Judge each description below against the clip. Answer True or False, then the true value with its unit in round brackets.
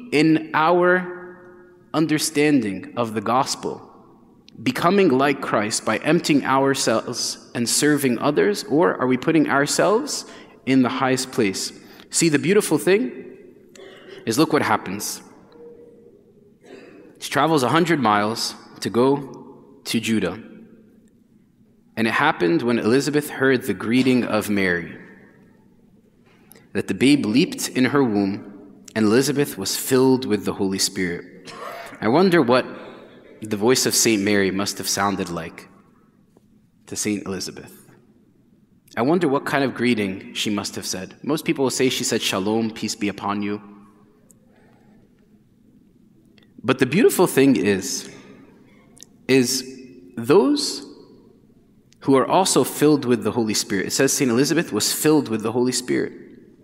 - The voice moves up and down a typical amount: False (6.0 semitones)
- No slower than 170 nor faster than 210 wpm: False (135 wpm)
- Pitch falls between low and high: False (125 Hz)